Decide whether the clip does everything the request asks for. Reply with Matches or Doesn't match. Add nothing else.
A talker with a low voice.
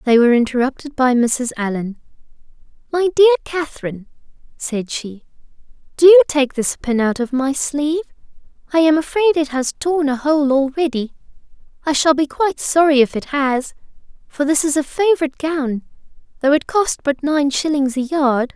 Doesn't match